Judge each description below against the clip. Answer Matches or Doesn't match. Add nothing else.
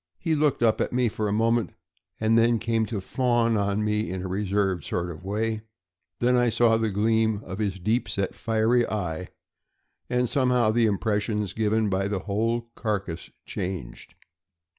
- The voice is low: Matches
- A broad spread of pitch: Doesn't match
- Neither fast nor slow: Matches